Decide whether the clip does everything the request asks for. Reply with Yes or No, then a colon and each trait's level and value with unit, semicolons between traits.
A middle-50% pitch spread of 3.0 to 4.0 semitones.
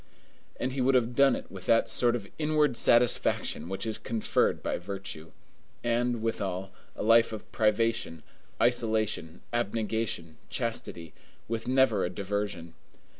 Yes: average, 3.7 semitones